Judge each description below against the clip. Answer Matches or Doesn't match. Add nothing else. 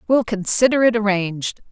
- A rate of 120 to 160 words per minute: Matches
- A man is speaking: Doesn't match